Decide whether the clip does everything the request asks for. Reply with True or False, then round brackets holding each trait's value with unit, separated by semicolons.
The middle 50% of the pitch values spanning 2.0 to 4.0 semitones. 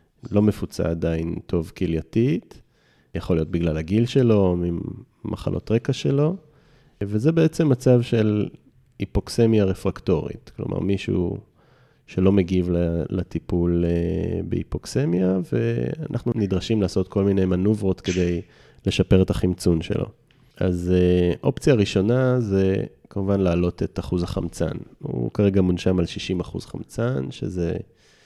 False (4.7 semitones)